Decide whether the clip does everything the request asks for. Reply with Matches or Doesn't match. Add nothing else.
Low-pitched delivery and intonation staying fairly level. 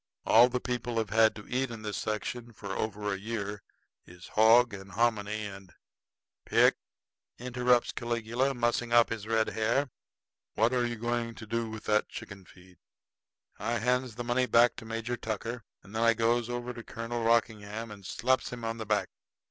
Matches